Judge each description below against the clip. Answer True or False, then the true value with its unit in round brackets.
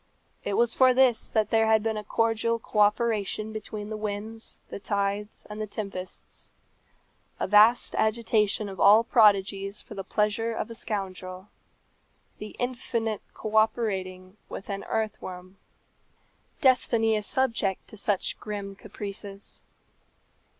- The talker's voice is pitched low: False (215 Hz)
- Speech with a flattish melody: True (2.1 semitones)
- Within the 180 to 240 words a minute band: False (135 wpm)